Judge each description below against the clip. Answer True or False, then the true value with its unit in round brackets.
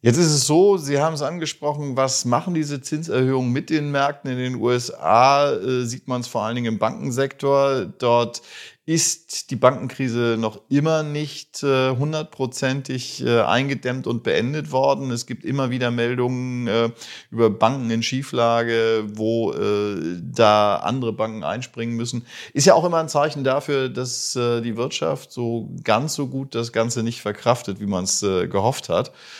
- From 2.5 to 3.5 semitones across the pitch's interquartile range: True (3.1 semitones)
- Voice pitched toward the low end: True (125 Hz)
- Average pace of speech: True (170 wpm)